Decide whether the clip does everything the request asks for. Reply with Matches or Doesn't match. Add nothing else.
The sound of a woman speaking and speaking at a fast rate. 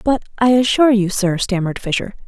Doesn't match